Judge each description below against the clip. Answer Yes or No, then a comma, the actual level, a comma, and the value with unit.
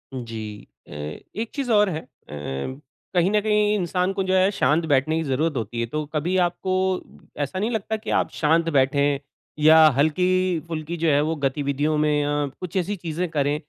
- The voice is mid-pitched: Yes, medium, 160 Hz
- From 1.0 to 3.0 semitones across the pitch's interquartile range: No, average, 4.4 semitones